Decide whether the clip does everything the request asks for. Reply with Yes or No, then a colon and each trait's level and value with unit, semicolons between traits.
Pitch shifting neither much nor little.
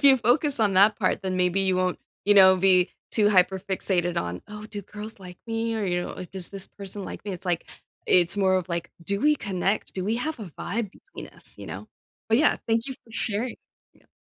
Yes: average, 3.3 semitones